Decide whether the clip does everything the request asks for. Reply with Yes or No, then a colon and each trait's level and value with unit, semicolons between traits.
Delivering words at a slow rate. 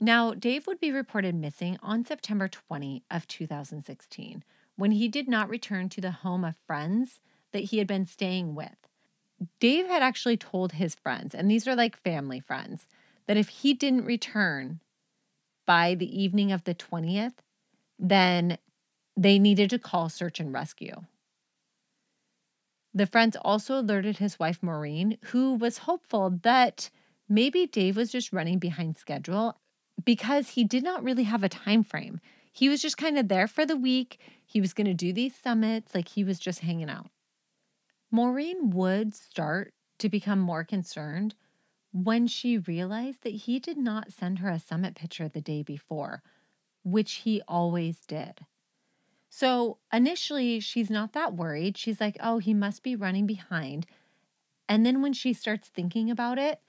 No: average, 165 wpm